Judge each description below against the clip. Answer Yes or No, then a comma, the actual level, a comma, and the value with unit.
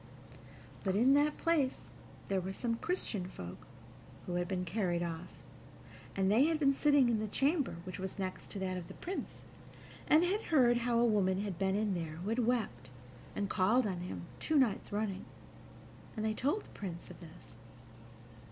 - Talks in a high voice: Yes, high, 205 Hz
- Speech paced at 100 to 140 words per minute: No, average, 185 wpm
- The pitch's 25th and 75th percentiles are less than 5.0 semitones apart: No, wide, 5.6 semitones